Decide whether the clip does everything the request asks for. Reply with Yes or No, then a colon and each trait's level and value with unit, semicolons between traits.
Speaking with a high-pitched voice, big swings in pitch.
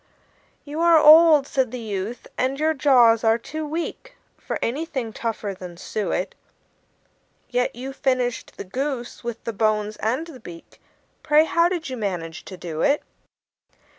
Yes: very high, 250 Hz; wide, 5.7 semitones